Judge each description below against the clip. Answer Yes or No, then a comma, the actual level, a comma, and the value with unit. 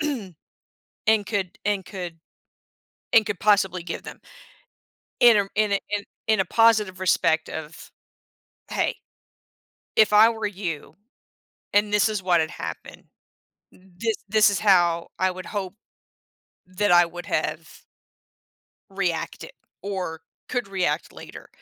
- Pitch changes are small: No, average, 3.0 semitones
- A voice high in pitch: Yes, high, 195 Hz